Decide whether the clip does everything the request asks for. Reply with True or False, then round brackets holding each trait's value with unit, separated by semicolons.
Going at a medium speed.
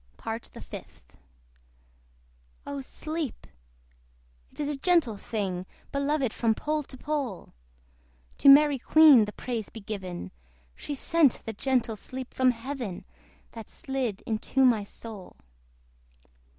False (125 wpm)